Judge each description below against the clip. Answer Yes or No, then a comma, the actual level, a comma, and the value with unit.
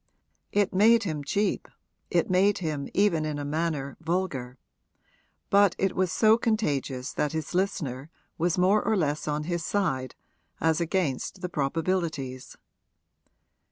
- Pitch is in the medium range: Yes, medium, 165 Hz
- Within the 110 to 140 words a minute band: Yes, slow, 135 wpm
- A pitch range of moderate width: Yes, average, 4.7 semitones